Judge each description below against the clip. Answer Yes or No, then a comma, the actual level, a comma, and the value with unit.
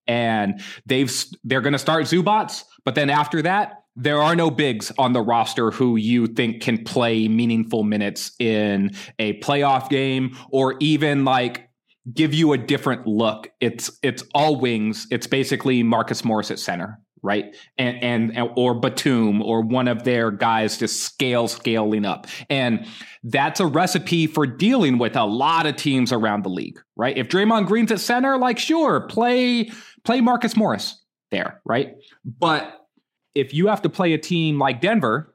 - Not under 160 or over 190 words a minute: Yes, average, 170 wpm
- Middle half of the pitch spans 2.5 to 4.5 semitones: No, wide, 5.5 semitones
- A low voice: Yes, low, 130 Hz